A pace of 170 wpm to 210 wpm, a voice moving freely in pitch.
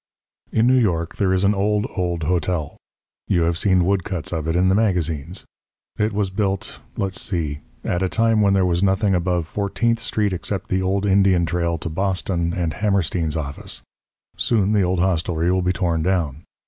No: average, 185 wpm; average, 2.7 semitones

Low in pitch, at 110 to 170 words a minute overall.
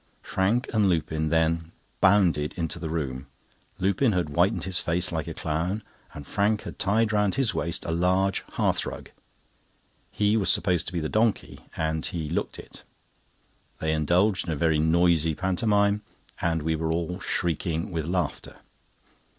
Yes: very low, 85 Hz; average, 160 wpm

